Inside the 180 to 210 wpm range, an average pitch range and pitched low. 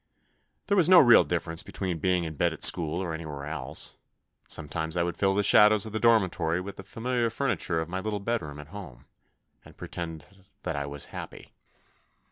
Yes: average, 200 wpm; average, 4.8 semitones; very low, 90 Hz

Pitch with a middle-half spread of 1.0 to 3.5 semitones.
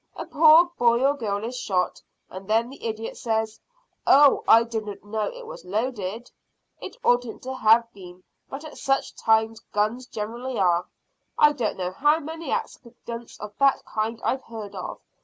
No: average, 3.9 semitones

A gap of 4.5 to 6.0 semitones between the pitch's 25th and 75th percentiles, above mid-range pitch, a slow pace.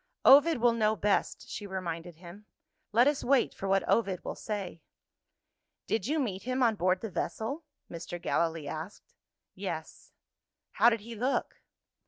No: average, 4.8 semitones; high, 210 Hz; average, 155 wpm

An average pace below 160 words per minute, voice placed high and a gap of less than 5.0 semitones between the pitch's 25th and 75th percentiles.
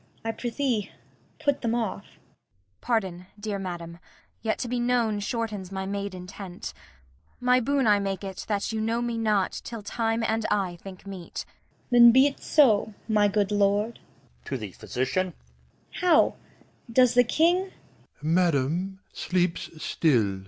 Yes: average, 140 wpm; high, 215 Hz; average, 3.6 semitones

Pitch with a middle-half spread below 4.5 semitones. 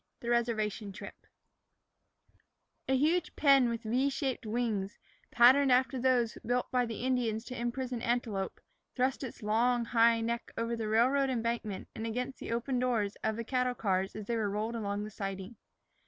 Yes: narrow, 2.5 semitones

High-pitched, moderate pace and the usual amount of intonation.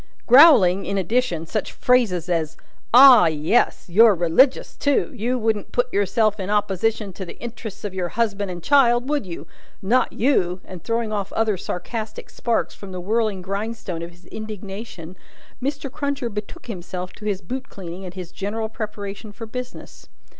Yes: high, 210 Hz; average, 165 wpm; average, 4.2 semitones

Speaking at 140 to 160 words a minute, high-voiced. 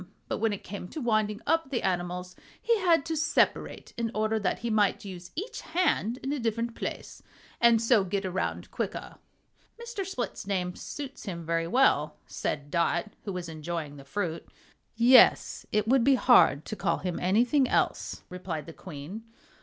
No: average, 175 wpm; high, 210 Hz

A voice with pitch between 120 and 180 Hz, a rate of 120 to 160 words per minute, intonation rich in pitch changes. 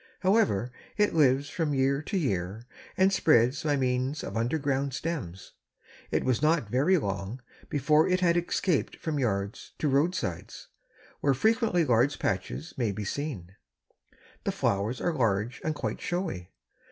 Yes: medium, 140 Hz; average, 145 wpm; wide, 6.2 semitones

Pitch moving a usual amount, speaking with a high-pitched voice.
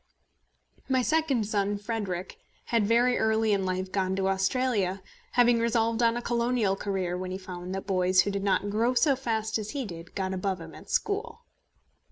Yes: average, 3.9 semitones; high, 205 Hz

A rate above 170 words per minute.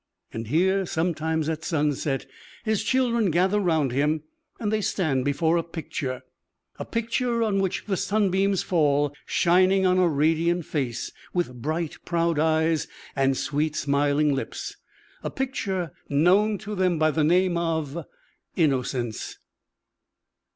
No: slow, 135 wpm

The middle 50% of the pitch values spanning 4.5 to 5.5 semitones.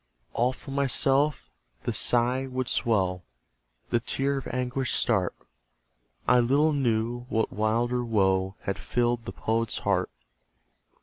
No: average, 2.7 semitones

